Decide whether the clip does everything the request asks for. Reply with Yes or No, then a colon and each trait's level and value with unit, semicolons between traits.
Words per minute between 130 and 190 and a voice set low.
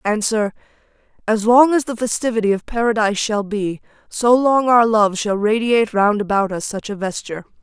No: average, 175 wpm; high, 215 Hz